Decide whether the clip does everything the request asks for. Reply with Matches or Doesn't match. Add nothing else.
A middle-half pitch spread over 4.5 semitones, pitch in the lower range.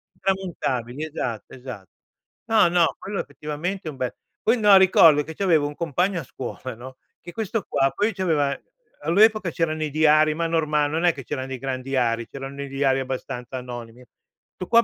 Doesn't match